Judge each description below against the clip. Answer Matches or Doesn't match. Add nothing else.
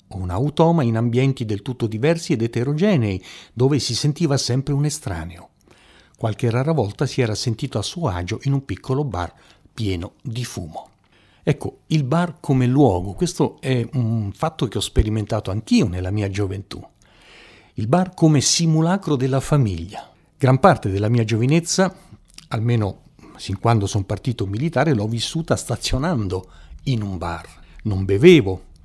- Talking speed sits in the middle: Matches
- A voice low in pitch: Matches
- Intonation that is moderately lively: Doesn't match